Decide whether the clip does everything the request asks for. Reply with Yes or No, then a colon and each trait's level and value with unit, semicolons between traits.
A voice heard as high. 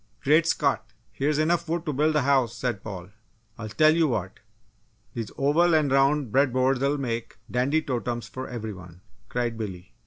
No: low, 130 Hz